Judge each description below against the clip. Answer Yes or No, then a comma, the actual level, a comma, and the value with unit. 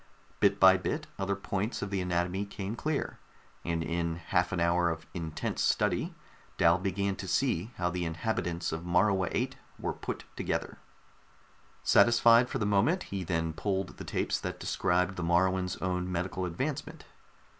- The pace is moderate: Yes, average, 160 wpm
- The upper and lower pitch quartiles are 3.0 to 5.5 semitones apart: No, narrow, 2.5 semitones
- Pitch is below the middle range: Yes, very low, 90 Hz